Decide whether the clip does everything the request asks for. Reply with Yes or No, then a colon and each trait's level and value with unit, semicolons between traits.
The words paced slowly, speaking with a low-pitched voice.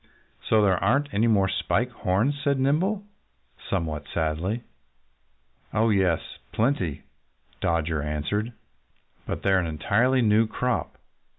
Yes: slow, 115 wpm; low, 105 Hz